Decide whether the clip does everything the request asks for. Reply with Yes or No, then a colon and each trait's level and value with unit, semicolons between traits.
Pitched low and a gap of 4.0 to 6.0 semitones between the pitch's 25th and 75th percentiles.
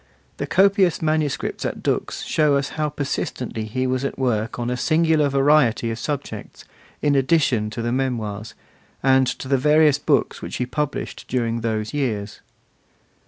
Yes: low, 130 Hz; average, 4.3 semitones